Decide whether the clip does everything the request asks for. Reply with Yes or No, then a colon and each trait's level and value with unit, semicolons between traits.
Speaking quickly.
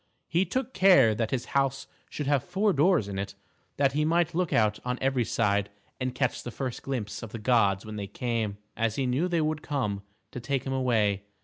Yes: fast, 215 wpm